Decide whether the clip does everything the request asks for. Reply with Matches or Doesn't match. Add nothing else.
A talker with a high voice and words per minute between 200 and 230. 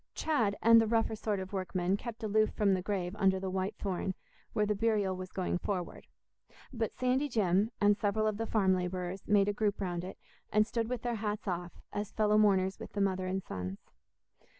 Matches